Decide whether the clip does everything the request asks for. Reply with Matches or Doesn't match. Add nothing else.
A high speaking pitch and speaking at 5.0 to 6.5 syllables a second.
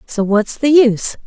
Doesn't match